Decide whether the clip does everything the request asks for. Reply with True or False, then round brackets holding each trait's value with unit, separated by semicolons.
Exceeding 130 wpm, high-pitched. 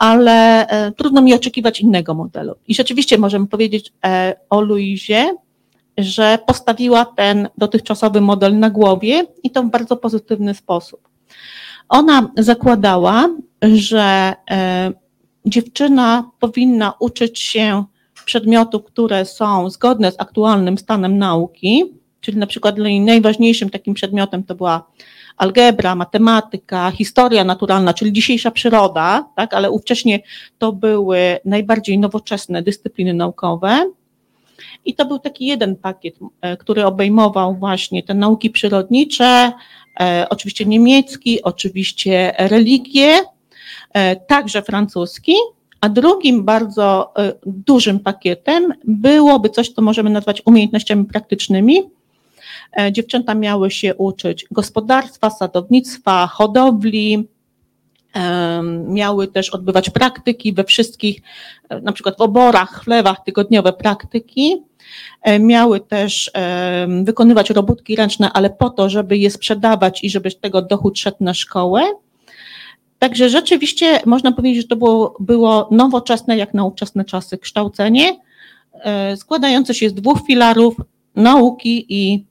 False (115 wpm; 215 Hz)